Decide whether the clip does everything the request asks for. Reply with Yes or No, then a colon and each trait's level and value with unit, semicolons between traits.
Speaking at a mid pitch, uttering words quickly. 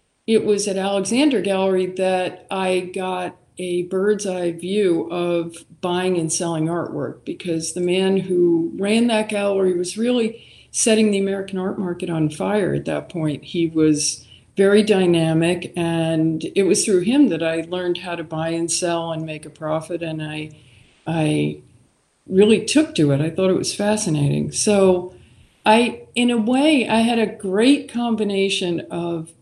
No: medium, 180 Hz; average, 160 wpm